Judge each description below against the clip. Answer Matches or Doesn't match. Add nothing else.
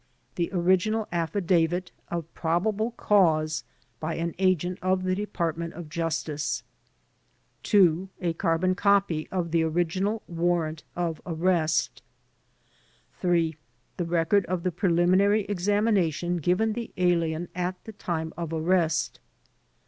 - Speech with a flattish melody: Matches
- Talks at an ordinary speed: Doesn't match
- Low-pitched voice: Doesn't match